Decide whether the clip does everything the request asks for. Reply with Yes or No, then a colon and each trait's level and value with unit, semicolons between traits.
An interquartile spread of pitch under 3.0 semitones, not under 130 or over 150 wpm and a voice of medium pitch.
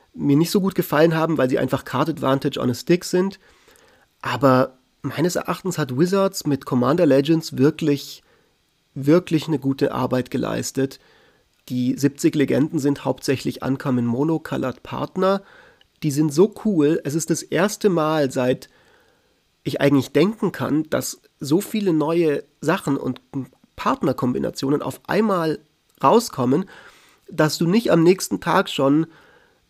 No: average, 4.5 semitones; average, 140 wpm; medium, 155 Hz